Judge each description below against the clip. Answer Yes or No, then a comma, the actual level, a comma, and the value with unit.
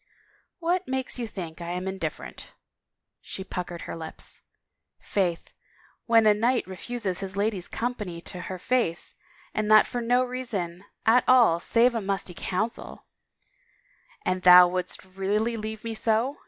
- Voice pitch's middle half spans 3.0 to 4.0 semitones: No, average, 4.6 semitones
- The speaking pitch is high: Yes, high, 210 Hz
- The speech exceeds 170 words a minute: No, average, 165 wpm